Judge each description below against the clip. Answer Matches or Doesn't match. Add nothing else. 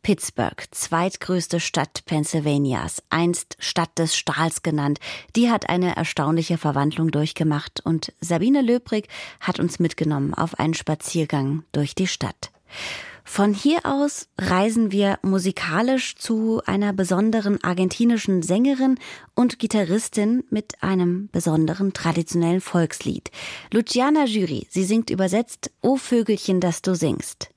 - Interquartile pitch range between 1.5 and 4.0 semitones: Doesn't match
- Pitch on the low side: Doesn't match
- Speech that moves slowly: Matches